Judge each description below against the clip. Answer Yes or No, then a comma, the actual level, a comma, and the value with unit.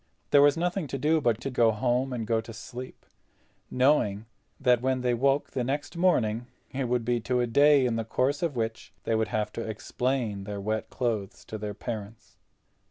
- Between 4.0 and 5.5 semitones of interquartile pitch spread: No, average, 3.4 semitones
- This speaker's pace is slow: No, average, 200 wpm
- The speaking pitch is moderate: No, low, 120 Hz